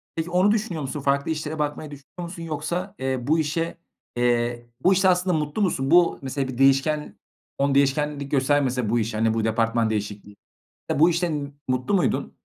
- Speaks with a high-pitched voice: No, medium, 145 Hz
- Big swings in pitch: No, average, 4.3 semitones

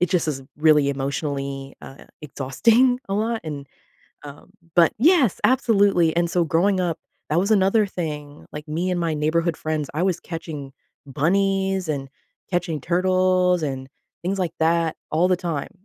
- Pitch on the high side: No, medium, 170 Hz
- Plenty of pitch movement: No, average, 3.9 semitones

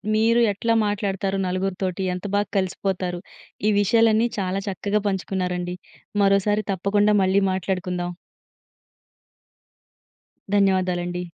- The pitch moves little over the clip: Yes, narrow, 2.0 semitones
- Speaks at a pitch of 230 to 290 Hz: No, high, 195 Hz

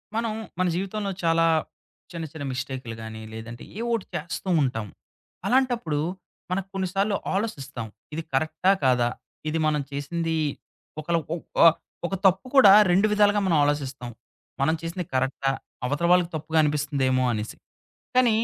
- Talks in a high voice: No, medium, 160 Hz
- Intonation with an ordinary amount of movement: No, wide, 6.1 semitones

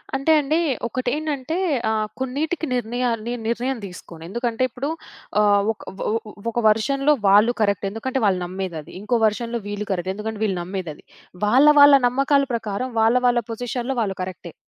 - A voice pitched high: Yes, high, 230 Hz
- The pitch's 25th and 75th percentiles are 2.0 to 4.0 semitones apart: No, average, 4.4 semitones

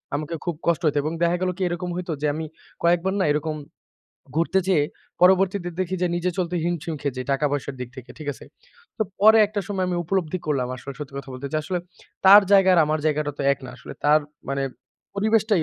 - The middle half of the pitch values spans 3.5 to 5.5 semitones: Yes, average, 4.0 semitones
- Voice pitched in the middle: Yes, medium, 170 Hz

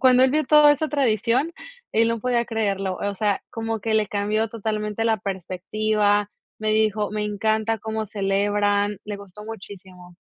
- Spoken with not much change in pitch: Yes, narrow, 1.8 semitones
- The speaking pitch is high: Yes, high, 215 Hz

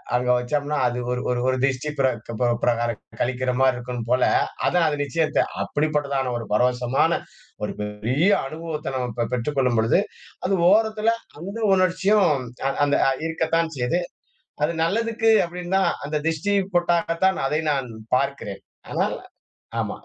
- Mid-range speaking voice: Yes, medium, 145 Hz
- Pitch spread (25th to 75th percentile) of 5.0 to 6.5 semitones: Yes, wide, 5.5 semitones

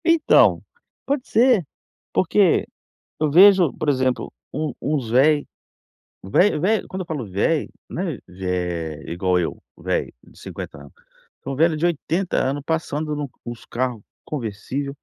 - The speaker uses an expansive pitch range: Yes, wide, 6.5 semitones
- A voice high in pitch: No, medium, 145 Hz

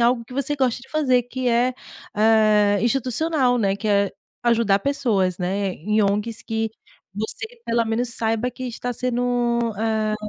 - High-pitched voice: Yes, high, 230 Hz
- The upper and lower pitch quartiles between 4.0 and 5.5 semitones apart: No, average, 2.9 semitones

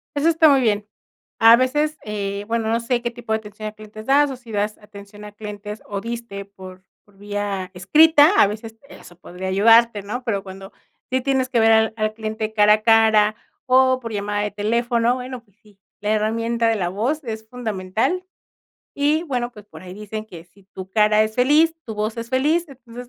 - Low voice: No, high, 220 Hz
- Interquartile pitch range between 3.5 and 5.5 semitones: No, average, 3.1 semitones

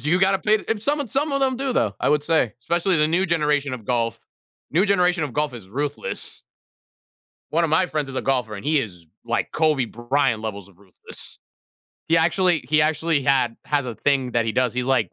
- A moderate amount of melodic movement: No, wide, 5.9 semitones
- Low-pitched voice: No, medium, 145 Hz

